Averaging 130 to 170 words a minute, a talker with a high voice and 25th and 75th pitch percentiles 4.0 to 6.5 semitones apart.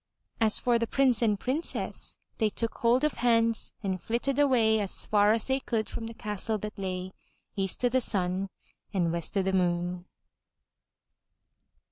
No: average, 165 wpm; high, 220 Hz; average, 3.6 semitones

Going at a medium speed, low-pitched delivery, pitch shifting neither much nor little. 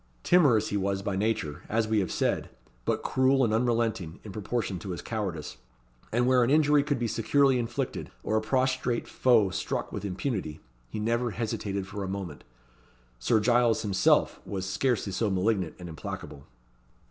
Yes: average, 170 wpm; low, 110 Hz; average, 4.0 semitones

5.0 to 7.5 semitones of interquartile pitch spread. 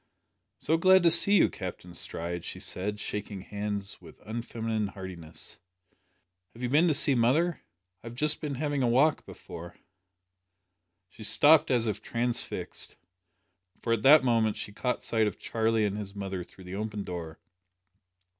Yes: wide, 5.5 semitones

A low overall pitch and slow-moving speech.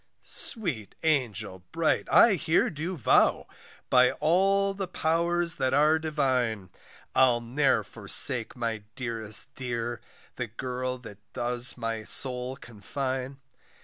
Yes: low, 130 Hz; slow, 115 wpm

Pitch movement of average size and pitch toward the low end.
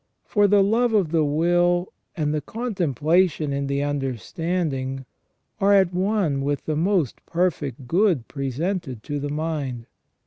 No: average, 4.8 semitones; medium, 160 Hz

